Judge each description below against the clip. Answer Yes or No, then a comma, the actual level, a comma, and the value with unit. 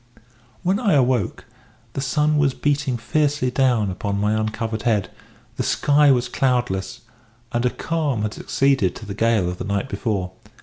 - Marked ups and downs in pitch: No, average, 4.8 semitones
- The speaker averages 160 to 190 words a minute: Yes, average, 165 wpm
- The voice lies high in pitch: No, low, 125 Hz